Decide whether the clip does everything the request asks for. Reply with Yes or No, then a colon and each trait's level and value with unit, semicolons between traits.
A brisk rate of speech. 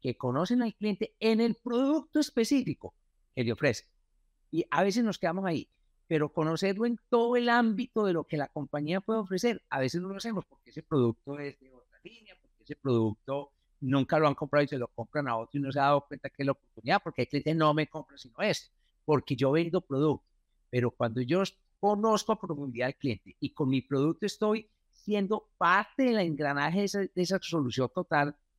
Yes: fast, 210 wpm